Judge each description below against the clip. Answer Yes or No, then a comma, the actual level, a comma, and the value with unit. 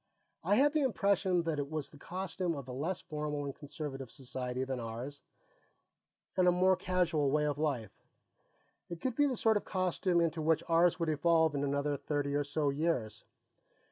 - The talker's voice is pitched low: No, medium, 155 Hz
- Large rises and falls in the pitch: No, average, 4.0 semitones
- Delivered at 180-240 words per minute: Yes, average, 185 wpm